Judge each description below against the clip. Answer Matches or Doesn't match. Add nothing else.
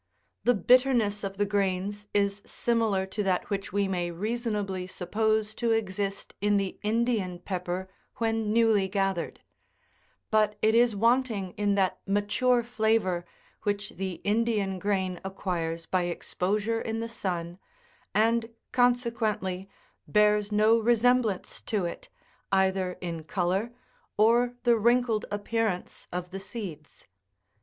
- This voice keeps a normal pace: Doesn't match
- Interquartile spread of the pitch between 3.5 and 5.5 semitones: Doesn't match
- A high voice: Matches